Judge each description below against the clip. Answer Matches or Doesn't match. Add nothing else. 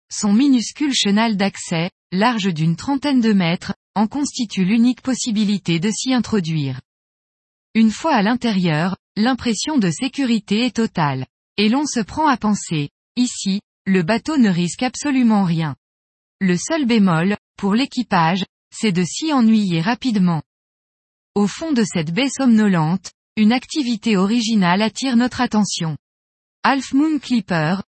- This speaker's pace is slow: Matches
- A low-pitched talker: Doesn't match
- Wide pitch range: Doesn't match